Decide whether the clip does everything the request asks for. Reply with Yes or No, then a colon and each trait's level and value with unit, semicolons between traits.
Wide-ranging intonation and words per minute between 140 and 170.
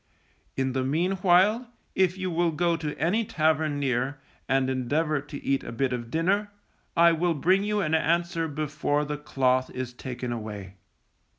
No: average, 4.7 semitones; average, 165 wpm